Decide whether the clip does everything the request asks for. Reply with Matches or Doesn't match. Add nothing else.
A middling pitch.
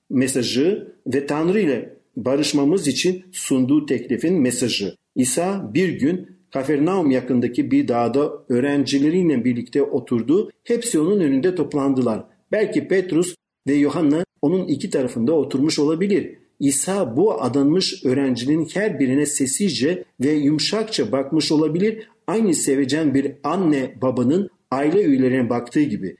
Matches